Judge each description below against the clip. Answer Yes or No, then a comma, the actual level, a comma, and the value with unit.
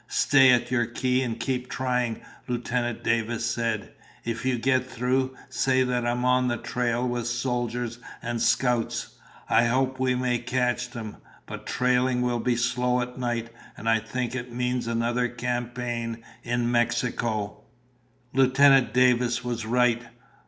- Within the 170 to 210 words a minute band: No, average, 145 wpm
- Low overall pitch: Yes, low, 120 Hz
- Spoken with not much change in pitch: Yes, narrow, 1.2 semitones